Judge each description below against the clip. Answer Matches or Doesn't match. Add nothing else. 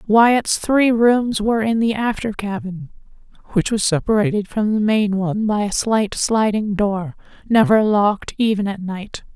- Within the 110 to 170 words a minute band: Matches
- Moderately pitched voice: Doesn't match